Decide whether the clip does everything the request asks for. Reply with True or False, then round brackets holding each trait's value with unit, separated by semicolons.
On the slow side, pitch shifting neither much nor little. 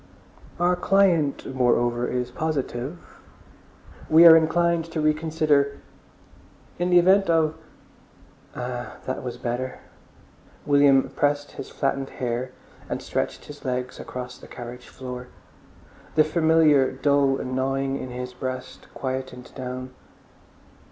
True (120 wpm; 3.9 semitones)